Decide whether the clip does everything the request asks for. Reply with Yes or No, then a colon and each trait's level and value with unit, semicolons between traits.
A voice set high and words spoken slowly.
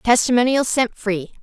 Yes: high, 230 Hz; slow, 125 wpm